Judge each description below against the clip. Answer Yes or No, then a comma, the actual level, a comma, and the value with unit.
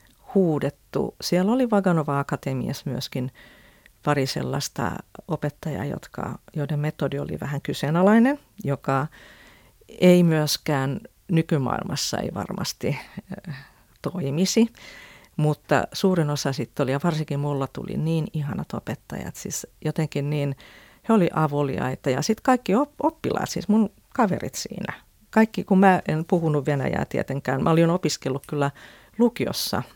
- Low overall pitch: No, medium, 155 Hz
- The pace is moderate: Yes, average, 120 wpm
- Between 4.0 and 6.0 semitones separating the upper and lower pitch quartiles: Yes, average, 4.6 semitones